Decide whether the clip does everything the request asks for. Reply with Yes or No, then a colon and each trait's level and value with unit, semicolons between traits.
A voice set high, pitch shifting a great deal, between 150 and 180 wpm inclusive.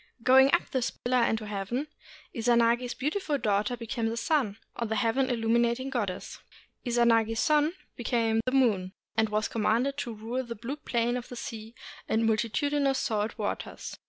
No: high, 235 Hz; narrow, 2.6 semitones; average, 160 wpm